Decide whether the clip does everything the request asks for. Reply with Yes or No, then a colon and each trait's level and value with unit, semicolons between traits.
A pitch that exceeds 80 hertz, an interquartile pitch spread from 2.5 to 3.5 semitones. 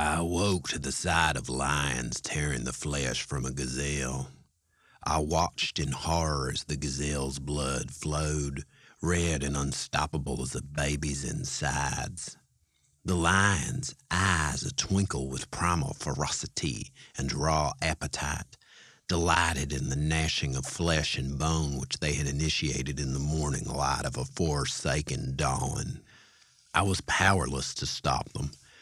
No: very low, 75 Hz; average, 2.9 semitones